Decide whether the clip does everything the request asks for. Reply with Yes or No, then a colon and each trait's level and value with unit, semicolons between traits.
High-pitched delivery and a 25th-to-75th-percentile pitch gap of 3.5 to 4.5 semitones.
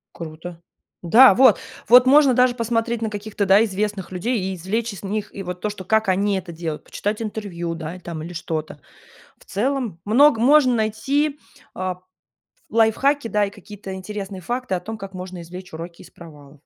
Yes: high, 200 Hz; average, 4.2 semitones